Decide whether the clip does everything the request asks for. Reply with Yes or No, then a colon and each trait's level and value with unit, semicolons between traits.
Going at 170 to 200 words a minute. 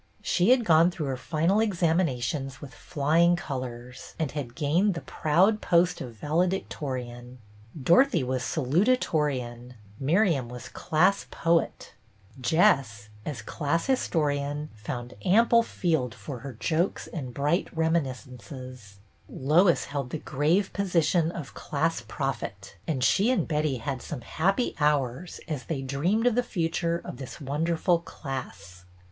No: slow, 135 wpm